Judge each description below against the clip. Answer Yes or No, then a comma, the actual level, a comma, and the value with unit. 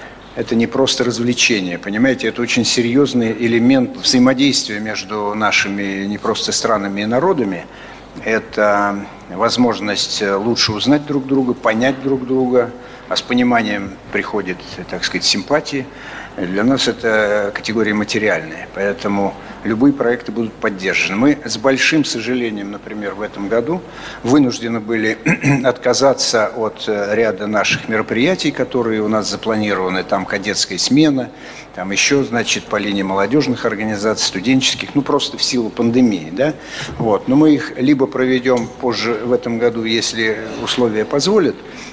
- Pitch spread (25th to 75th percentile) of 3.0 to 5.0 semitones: Yes, average, 3.7 semitones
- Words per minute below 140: Yes, average, 130 wpm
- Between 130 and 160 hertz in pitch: No, low, 120 Hz